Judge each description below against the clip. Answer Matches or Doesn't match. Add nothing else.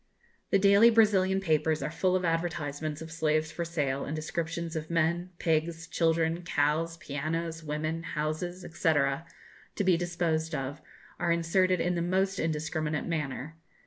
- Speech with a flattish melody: Matches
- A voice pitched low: Doesn't match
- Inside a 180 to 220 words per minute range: Doesn't match